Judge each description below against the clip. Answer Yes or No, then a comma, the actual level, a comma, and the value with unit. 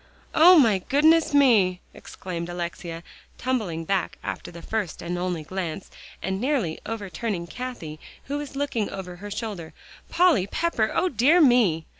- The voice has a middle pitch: No, high, 205 Hz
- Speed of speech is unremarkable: Yes, average, 145 wpm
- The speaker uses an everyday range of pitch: No, wide, 7.2 semitones